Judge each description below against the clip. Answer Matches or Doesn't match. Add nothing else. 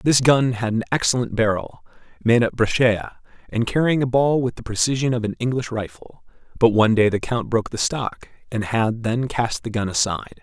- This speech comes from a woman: Doesn't match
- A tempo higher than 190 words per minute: Matches